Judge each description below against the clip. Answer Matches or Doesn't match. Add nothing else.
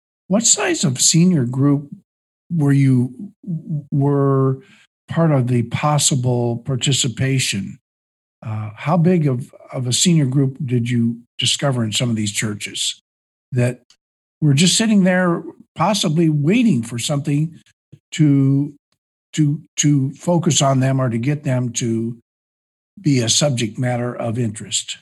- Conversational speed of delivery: Doesn't match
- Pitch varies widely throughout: Doesn't match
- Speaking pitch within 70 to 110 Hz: Doesn't match